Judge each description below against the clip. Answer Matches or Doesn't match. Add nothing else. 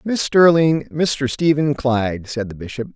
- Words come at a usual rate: Matches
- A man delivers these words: Matches